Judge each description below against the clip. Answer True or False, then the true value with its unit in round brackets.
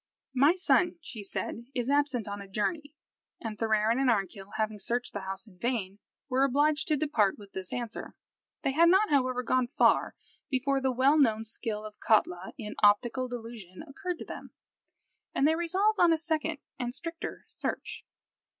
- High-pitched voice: True (250 Hz)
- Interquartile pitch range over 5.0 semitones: True (5.5 semitones)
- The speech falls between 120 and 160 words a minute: False (175 wpm)